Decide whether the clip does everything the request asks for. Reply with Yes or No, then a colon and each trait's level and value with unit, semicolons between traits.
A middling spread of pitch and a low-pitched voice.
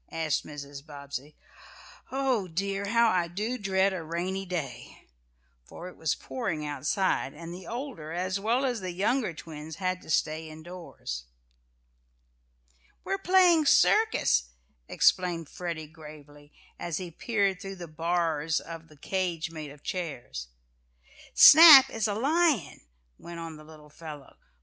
No: average, 4.5 semitones; medium, 170 Hz